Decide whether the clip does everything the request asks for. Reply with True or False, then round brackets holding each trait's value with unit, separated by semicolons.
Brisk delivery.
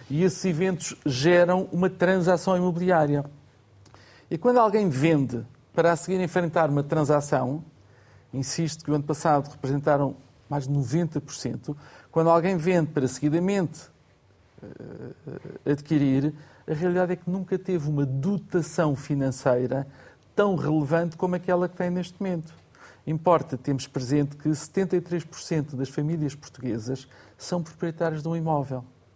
False (130 wpm)